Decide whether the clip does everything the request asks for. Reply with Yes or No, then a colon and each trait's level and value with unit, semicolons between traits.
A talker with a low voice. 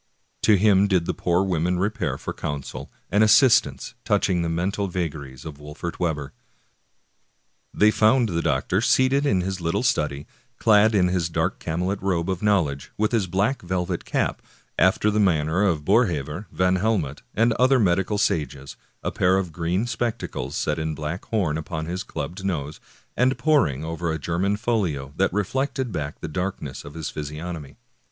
Yes: very low, 90 Hz